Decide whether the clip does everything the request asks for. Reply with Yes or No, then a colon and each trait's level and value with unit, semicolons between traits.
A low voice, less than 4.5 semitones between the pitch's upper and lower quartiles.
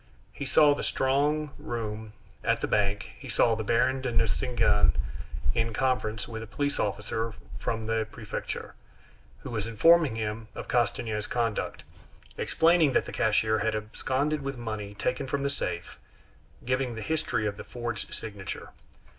Yes: low, 115 Hz; average, 3.5 semitones